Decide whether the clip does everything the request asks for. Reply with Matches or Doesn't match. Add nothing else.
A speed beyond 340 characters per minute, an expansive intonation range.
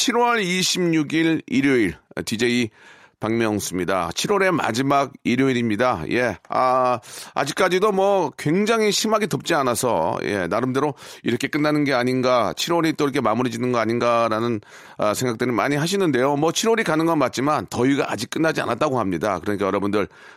Matches